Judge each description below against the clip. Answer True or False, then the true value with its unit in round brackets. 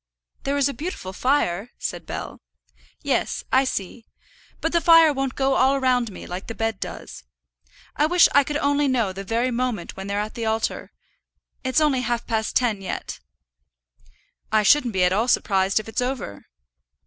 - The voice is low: False (245 Hz)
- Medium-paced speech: True (170 wpm)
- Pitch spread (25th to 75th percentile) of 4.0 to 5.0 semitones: True (4.6 semitones)